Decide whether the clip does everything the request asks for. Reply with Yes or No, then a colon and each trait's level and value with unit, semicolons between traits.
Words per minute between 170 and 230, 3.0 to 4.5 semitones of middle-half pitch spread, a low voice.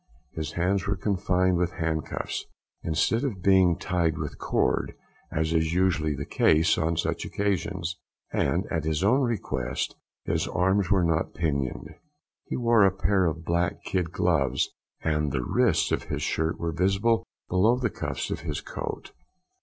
No: average, 160 wpm; average, 3.4 semitones; very low, 85 Hz